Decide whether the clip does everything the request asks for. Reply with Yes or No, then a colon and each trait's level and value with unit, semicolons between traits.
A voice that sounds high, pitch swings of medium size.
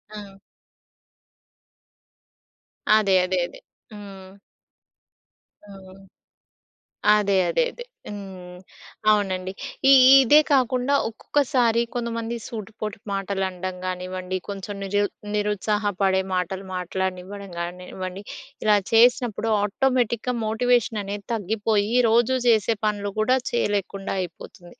Yes: high, 205 Hz; average, 3.2 semitones